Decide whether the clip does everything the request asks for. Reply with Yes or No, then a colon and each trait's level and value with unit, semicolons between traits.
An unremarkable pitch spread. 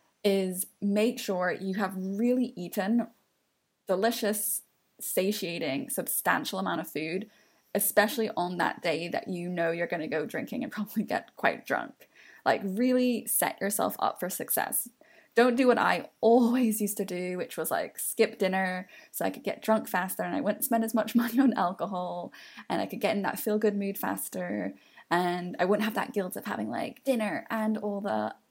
Yes: average, 4.0 semitones